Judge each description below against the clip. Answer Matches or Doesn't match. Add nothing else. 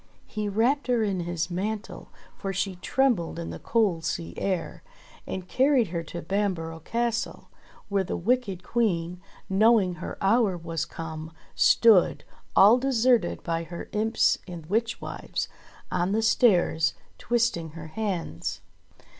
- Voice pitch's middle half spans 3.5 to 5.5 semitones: Matches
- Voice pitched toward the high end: Matches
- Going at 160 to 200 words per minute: Doesn't match